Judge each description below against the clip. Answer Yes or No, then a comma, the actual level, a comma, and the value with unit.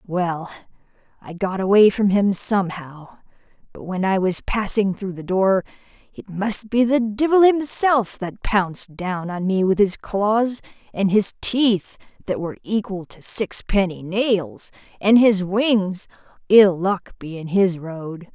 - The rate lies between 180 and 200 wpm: No, average, 150 wpm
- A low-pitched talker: No, high, 195 Hz